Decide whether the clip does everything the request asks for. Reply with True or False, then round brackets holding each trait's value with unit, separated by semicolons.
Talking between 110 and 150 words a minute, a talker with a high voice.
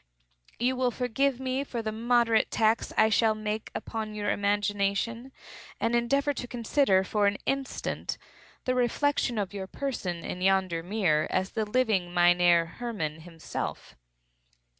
True (140 wpm; 220 Hz)